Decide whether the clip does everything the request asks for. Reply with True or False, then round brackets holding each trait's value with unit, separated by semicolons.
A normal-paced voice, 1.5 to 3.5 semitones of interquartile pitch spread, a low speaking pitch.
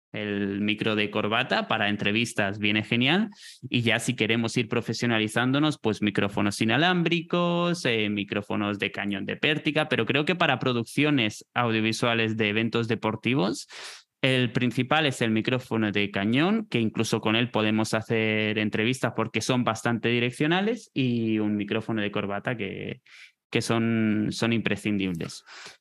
True (140 wpm; 3.1 semitones; 115 Hz)